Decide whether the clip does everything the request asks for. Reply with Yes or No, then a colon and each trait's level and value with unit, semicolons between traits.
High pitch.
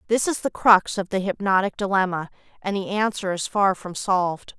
Yes: high, 195 Hz